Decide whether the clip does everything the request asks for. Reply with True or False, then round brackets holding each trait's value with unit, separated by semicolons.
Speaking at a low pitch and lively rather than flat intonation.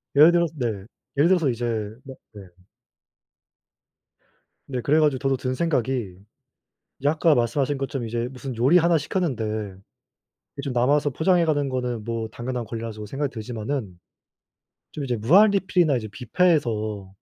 False (130 Hz; 4.5 semitones)